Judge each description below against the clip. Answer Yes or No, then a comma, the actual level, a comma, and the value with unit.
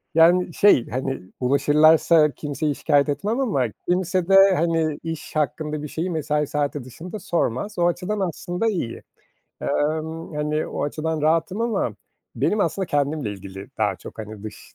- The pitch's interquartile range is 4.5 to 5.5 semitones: No, average, 3.7 semitones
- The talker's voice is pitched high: No, medium, 155 Hz